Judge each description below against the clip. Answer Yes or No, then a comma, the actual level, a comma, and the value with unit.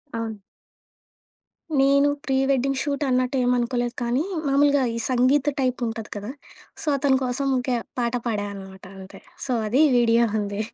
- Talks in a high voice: Yes, very high, 250 Hz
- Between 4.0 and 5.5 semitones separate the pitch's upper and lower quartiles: No, average, 2.8 semitones